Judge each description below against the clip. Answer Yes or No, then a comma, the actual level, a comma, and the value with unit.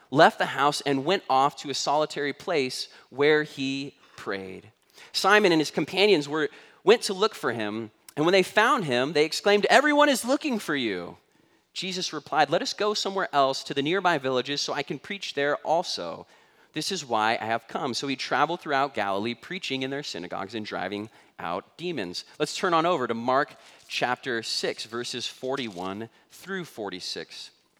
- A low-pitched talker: No, medium, 145 Hz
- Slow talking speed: No, average, 180 wpm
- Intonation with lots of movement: Yes, wide, 7.1 semitones